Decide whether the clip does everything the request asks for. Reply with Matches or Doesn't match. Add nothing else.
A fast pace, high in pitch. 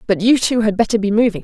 Matches